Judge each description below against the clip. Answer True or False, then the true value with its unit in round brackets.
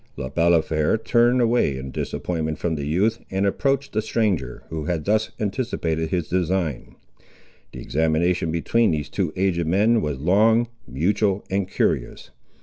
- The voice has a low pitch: True (90 Hz)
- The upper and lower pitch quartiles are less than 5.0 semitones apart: False (5.4 semitones)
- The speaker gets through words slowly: False (145 wpm)